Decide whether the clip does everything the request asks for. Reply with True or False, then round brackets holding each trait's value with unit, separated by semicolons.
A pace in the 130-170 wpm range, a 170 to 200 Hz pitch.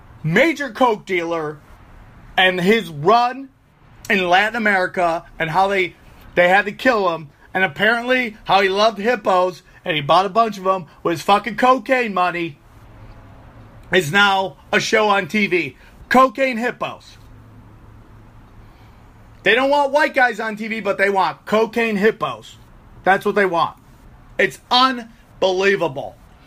True (140 wpm; 190 Hz)